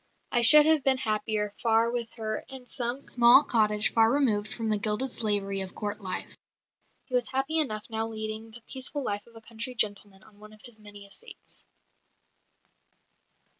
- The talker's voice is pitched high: Yes, high, 225 Hz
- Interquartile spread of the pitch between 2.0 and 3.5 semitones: Yes, average, 2.8 semitones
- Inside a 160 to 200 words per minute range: Yes, average, 175 wpm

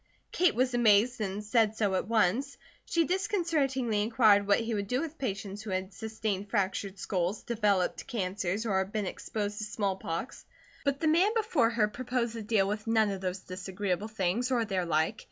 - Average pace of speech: Yes, average, 180 wpm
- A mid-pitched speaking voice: No, high, 215 Hz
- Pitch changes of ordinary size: Yes, average, 3.5 semitones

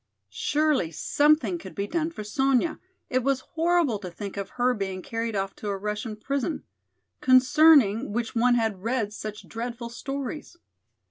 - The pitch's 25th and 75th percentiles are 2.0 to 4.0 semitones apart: No, average, 5.2 semitones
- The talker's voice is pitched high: Yes, high, 240 Hz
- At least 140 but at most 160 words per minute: Yes, average, 155 wpm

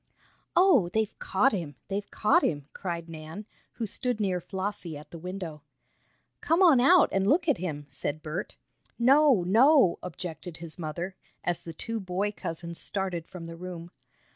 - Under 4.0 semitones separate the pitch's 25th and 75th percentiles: No, average, 4.7 semitones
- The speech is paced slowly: No, average, 165 wpm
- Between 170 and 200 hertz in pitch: Yes, medium, 185 Hz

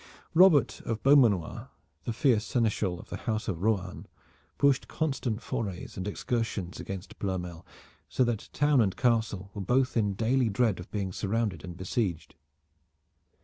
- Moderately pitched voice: No, low, 110 Hz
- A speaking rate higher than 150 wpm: No, average, 145 wpm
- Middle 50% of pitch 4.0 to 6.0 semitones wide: Yes, average, 4.5 semitones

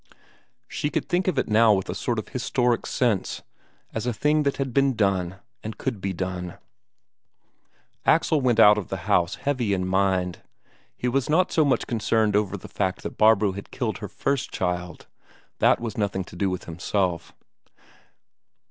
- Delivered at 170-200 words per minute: Yes, average, 175 wpm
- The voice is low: Yes, low, 105 Hz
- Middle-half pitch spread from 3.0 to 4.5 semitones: No, average, 5.2 semitones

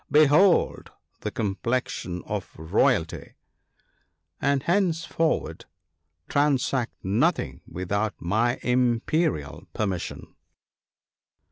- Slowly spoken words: Yes, slow, 75 wpm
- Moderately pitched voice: No, low, 120 Hz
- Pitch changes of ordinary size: No, wide, 7.6 semitones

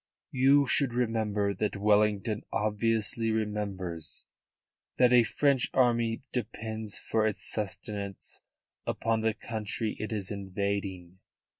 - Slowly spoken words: Yes, slow, 110 wpm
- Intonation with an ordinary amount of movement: No, narrow, 2.1 semitones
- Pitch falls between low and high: No, low, 110 Hz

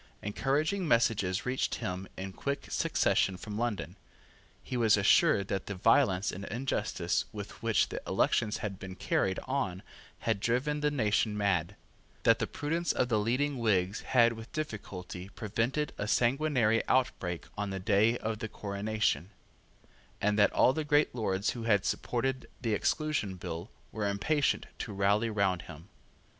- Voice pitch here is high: No, low, 110 Hz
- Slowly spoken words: No, average, 155 wpm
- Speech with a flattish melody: No, average, 4.3 semitones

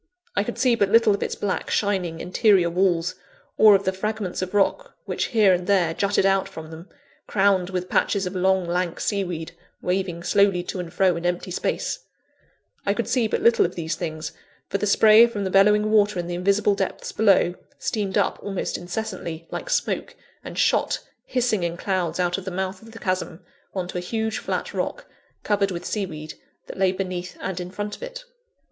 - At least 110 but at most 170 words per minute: No, fast, 205 wpm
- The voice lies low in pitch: No, high, 190 Hz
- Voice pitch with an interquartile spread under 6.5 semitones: Yes, narrow, 2.6 semitones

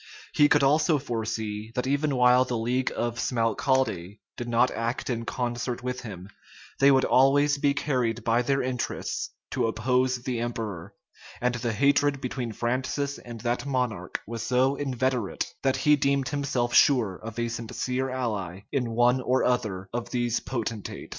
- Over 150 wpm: Yes, average, 160 wpm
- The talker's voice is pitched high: No, low, 125 Hz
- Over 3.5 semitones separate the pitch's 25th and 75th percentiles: No, narrow, 2.4 semitones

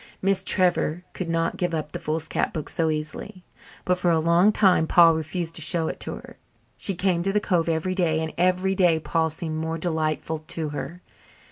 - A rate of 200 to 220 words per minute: Yes, fast, 205 wpm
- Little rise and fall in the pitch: Yes, narrow, 2.3 semitones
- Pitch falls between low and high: Yes, medium, 165 Hz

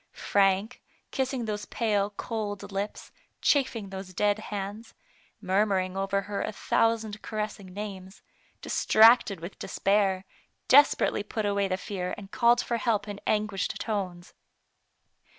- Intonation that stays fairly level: Yes, narrow, 2.0 semitones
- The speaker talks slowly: Yes, slow, 130 wpm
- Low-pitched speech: No, high, 205 Hz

